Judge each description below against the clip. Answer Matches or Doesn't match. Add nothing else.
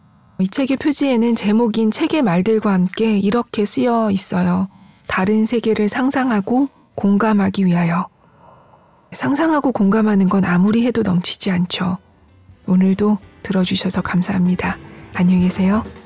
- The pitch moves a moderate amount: Matches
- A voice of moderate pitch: Doesn't match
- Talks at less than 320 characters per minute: Matches